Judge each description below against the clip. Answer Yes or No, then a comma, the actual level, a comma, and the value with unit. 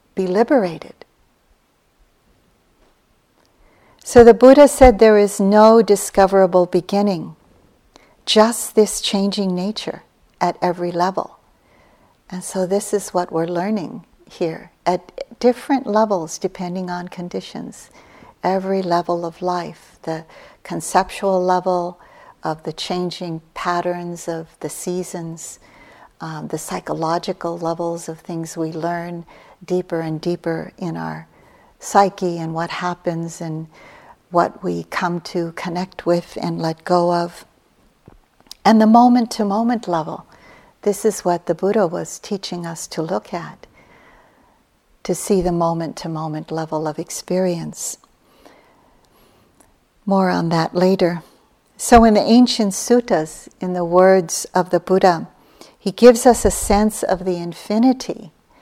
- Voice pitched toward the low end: No, medium, 180 Hz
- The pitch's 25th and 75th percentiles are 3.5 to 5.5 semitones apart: No, average, 3.1 semitones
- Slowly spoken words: Yes, slow, 125 wpm